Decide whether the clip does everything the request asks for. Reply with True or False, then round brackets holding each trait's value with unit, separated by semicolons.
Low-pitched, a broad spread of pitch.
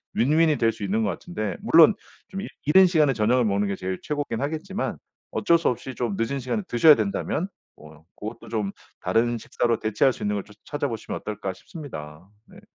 True (120 Hz; 6.7 semitones)